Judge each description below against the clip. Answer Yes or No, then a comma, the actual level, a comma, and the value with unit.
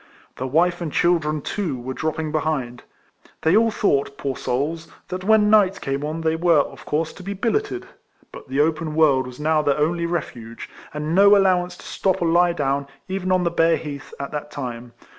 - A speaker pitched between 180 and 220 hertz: No, medium, 160 Hz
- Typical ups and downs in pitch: Yes, average, 4.0 semitones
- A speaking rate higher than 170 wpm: Yes, average, 200 wpm